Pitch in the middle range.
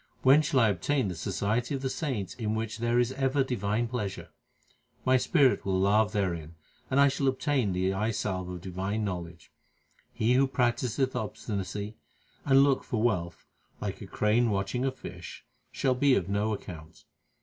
No: low, 110 Hz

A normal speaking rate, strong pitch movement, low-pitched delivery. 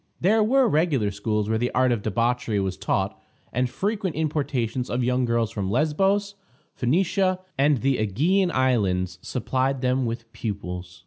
Yes: average, 150 wpm; wide, 6.0 semitones; low, 125 Hz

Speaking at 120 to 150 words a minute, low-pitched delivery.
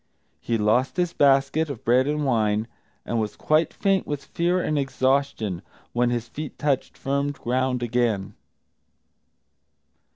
Yes: slow, 135 wpm; low, 130 Hz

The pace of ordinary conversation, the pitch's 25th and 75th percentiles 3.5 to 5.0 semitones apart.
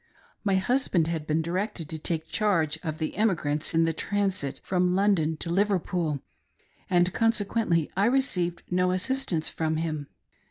Yes: average, 155 wpm; average, 3.9 semitones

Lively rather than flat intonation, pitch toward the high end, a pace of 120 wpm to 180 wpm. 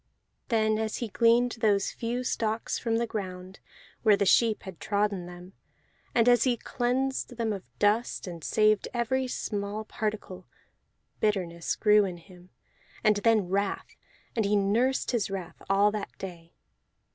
No: average, 3.0 semitones; high, 210 Hz; average, 150 wpm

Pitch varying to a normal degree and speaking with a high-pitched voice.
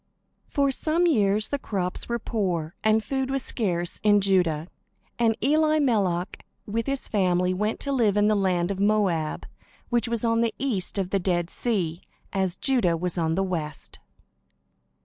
Yes: average, 4.6 semitones; high, 205 Hz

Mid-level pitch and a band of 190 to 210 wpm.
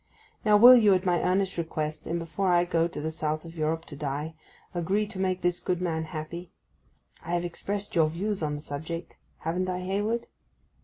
Yes: medium, 175 Hz; average, 200 wpm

